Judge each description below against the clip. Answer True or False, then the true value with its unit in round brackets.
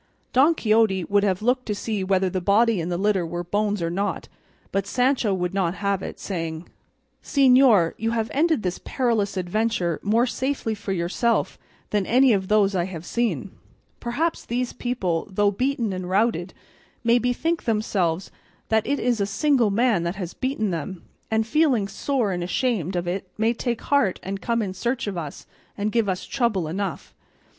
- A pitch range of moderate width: True (4.3 semitones)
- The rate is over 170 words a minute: True (180 wpm)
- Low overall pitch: False (205 Hz)